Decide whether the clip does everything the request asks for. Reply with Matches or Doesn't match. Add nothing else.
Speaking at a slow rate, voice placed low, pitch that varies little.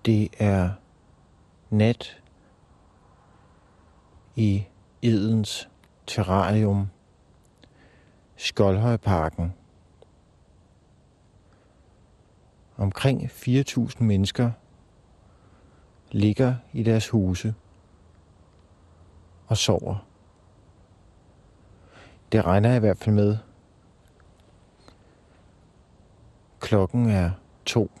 Doesn't match